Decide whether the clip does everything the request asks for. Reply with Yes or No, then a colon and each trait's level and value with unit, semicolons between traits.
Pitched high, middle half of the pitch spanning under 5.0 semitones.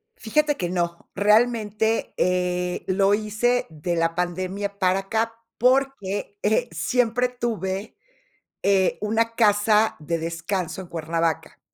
Yes: high, 200 Hz; average, 4.0 semitones